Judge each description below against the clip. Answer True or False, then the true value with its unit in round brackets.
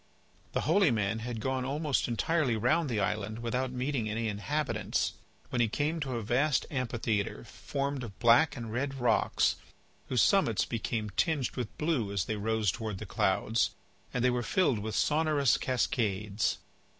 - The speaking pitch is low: True (120 Hz)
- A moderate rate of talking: True (160 wpm)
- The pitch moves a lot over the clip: False (4.2 semitones)